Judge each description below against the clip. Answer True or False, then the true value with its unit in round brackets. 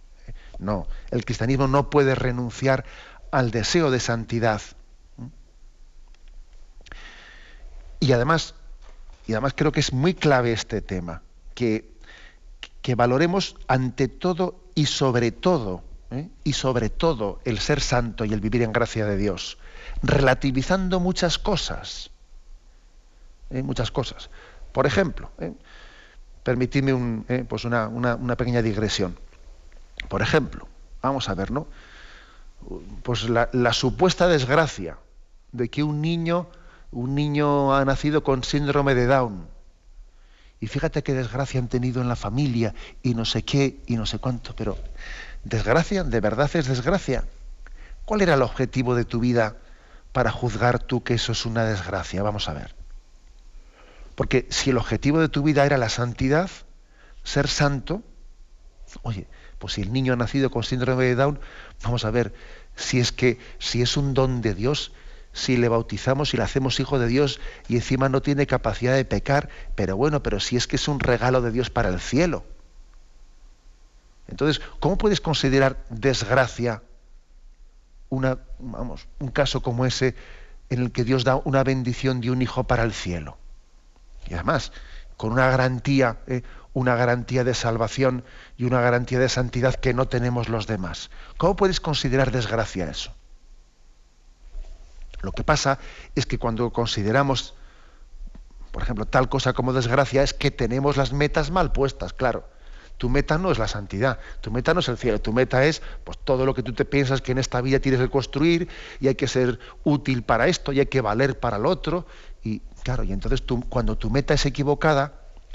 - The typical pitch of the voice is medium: False (125 Hz)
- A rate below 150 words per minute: False (165 wpm)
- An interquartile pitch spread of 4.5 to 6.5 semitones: False (3.3 semitones)